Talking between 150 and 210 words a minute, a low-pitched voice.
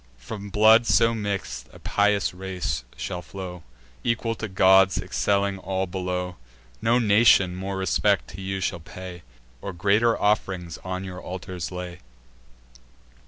No: slow, 135 wpm; very low, 95 Hz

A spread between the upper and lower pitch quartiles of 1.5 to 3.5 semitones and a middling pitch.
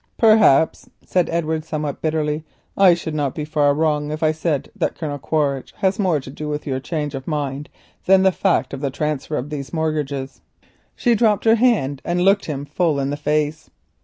Yes: average, 3.0 semitones; medium, 155 Hz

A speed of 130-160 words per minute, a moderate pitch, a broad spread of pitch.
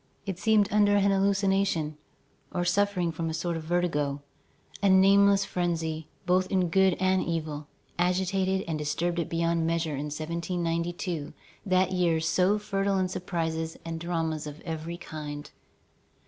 No: average, 145 wpm; medium, 175 Hz; average, 2.8 semitones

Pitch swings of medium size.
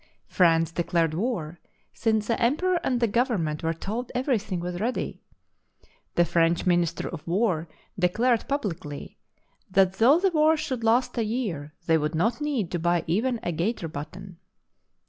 No: wide, 6.2 semitones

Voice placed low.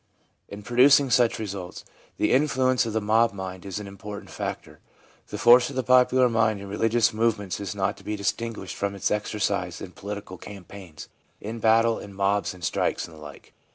Yes: low, 105 Hz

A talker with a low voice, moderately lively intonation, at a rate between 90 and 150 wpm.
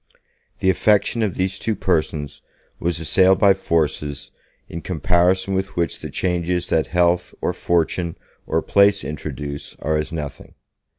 Yes: very low, 85 Hz; average, 3.2 semitones; average, 140 wpm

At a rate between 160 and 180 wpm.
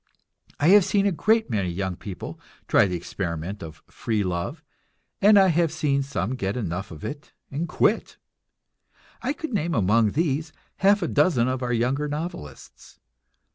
Yes: average, 165 wpm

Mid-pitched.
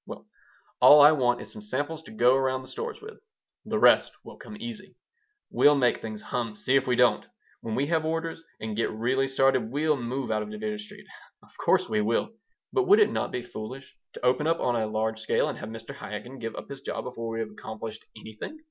No: low, 130 Hz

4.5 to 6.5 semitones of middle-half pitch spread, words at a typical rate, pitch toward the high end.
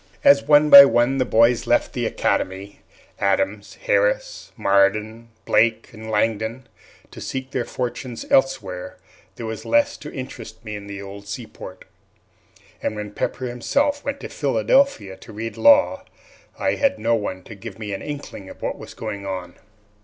No: average, 5.2 semitones; average, 160 wpm; low, 115 Hz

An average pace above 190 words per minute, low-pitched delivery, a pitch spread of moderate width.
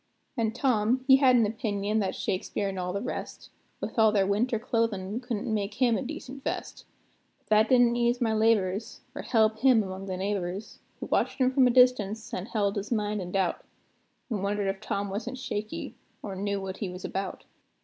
No: average, 200 wpm; high, 215 Hz; average, 3.2 semitones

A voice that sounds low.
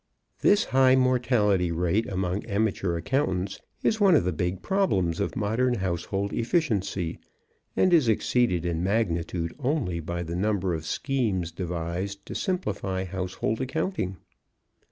Yes: low, 100 Hz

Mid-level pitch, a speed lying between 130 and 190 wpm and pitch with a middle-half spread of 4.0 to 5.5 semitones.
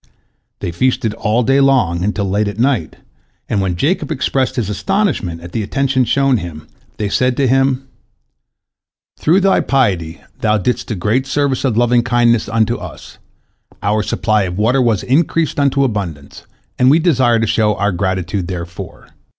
No: low, 115 Hz; average, 160 wpm; average, 4.9 semitones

